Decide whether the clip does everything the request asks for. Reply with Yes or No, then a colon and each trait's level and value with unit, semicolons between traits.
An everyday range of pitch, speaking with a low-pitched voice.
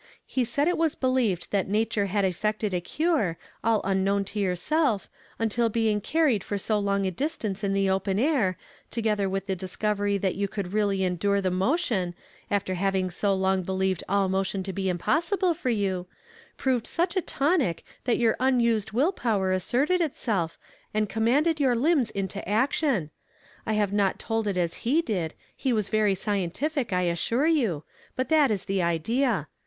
No: average, 4.7 semitones; high, 205 Hz